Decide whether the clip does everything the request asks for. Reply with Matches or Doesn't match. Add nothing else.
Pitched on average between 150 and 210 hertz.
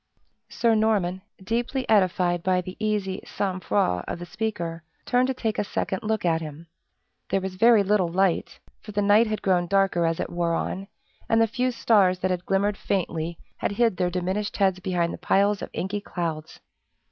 Matches